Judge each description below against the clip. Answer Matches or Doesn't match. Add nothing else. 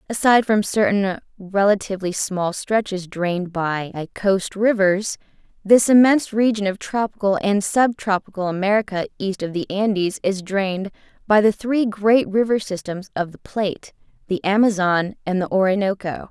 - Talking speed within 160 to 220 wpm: Doesn't match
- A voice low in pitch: Doesn't match